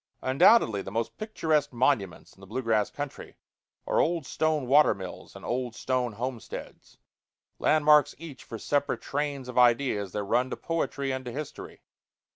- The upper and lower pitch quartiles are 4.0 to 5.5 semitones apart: Yes, average, 4.3 semitones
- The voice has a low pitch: Yes, low, 130 Hz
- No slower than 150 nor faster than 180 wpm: Yes, average, 160 wpm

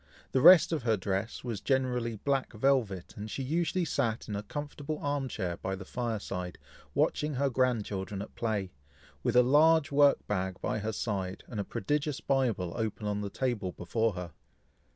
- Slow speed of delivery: No, average, 180 wpm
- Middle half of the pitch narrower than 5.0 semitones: No, wide, 5.5 semitones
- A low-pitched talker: Yes, low, 115 Hz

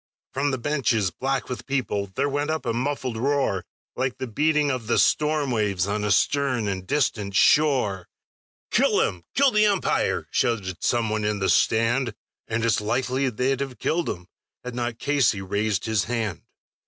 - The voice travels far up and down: No, average, 4.8 semitones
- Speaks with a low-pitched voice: Yes, low, 120 Hz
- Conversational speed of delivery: Yes, average, 175 wpm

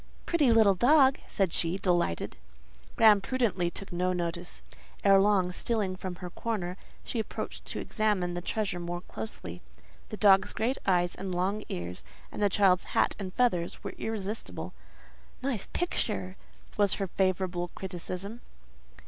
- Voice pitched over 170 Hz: Yes, high, 190 Hz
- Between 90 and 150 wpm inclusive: Yes, average, 145 wpm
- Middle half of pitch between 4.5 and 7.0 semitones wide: No, average, 3.3 semitones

